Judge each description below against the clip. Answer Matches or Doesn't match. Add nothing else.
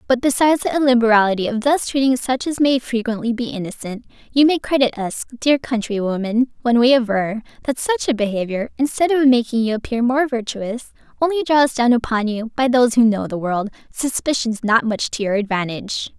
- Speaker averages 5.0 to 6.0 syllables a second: Matches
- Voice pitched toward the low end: Doesn't match